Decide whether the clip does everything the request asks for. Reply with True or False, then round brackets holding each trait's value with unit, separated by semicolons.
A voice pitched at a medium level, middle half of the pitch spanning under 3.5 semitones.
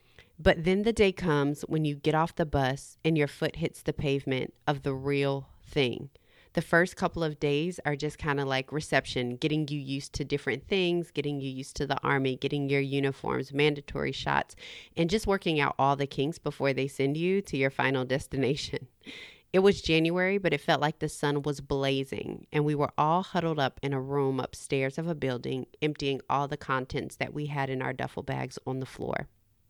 True (145 Hz; 2.6 semitones)